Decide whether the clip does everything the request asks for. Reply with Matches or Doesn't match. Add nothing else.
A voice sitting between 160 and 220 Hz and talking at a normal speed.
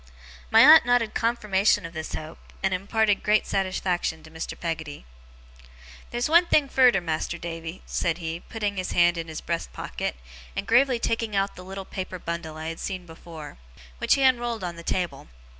Matches